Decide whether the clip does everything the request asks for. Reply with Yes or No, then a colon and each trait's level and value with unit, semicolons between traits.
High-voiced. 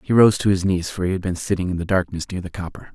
No: very low, 90 Hz